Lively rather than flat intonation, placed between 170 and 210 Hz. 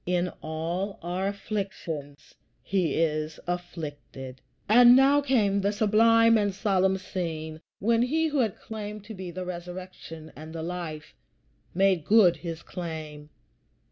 No: average, 4.5 semitones; medium, 185 Hz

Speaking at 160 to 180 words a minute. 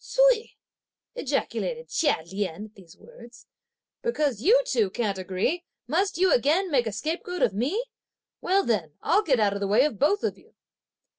Yes: average, 170 wpm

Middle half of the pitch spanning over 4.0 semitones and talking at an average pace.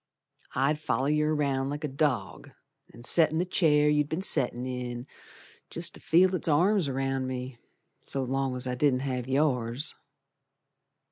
No: average, 3.1 semitones; average, 155 wpm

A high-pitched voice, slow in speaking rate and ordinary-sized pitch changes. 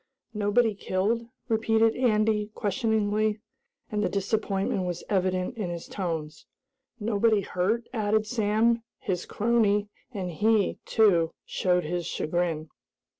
Yes: high, 205 Hz; slow, 115 wpm; average, 3.3 semitones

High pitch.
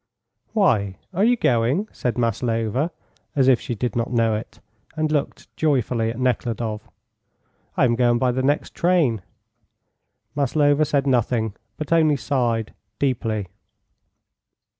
No: low, 125 Hz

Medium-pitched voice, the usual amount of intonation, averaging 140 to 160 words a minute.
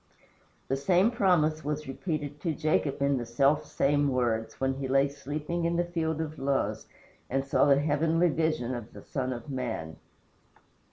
No: medium, 145 Hz; average, 3.0 semitones; average, 170 wpm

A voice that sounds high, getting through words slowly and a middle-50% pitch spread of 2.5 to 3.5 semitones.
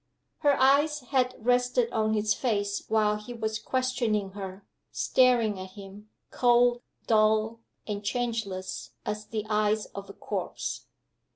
Yes: high, 220 Hz; slow, 130 wpm; average, 2.9 semitones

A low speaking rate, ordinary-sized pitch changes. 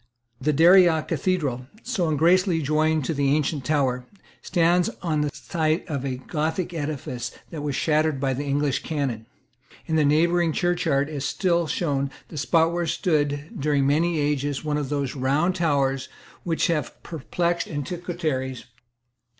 No: average, 150 wpm; average, 3.2 semitones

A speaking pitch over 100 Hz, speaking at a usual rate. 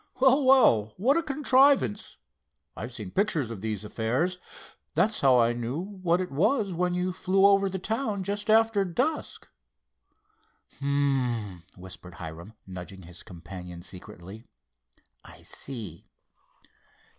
No: medium, 140 Hz; slow, 125 wpm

